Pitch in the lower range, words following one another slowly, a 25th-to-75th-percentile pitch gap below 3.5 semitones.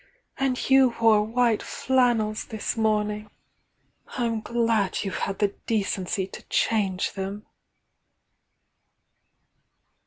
No: high, 215 Hz; slow, 115 wpm; narrow, 2.4 semitones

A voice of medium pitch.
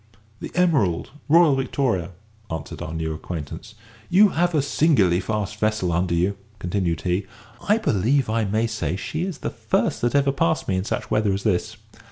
No: low, 105 Hz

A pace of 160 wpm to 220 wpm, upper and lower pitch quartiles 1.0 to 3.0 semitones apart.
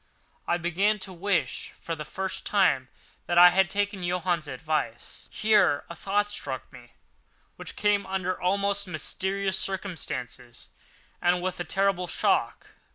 No: average, 140 wpm; narrow, 2.5 semitones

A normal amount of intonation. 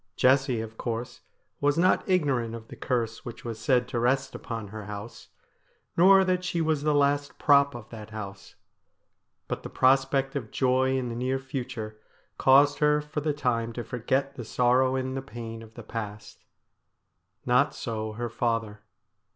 Yes: average, 3.6 semitones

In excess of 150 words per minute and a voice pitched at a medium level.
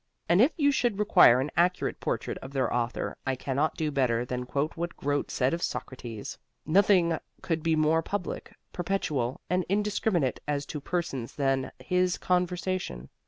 Yes: average, 165 wpm; medium, 155 Hz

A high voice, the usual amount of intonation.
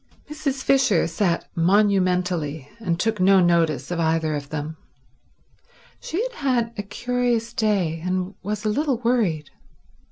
No: high, 195 Hz; wide, 5.9 semitones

